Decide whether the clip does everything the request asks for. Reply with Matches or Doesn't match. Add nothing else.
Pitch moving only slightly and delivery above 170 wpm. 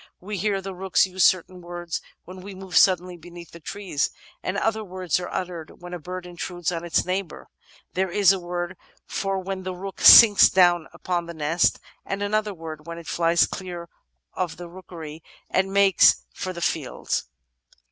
Matches